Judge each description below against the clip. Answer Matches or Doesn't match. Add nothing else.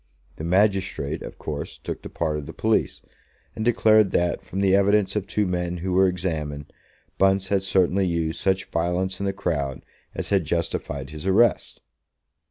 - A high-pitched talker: Doesn't match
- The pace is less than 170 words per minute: Doesn't match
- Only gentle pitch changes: Doesn't match